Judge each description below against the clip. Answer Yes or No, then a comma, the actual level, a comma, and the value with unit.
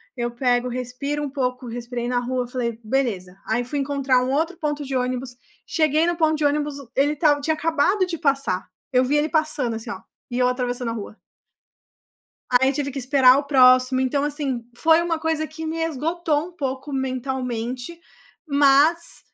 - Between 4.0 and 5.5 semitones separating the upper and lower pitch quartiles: No, average, 3.3 semitones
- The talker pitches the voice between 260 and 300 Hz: Yes, very high, 270 Hz